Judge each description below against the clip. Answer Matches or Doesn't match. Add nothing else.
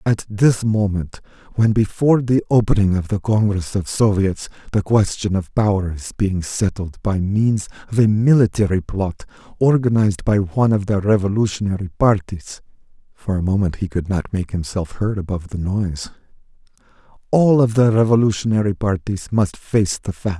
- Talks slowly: Doesn't match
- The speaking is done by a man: Matches